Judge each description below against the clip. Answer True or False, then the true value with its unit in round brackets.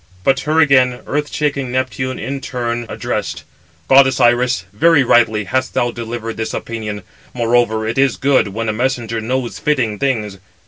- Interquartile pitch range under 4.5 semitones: True (2.7 semitones)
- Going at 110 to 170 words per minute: True (155 wpm)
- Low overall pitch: True (120 Hz)